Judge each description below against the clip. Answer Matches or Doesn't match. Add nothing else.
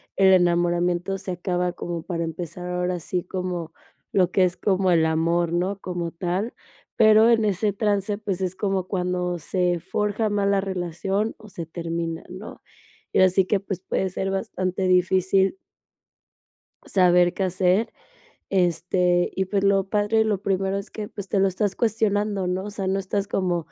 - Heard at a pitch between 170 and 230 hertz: Matches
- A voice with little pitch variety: Matches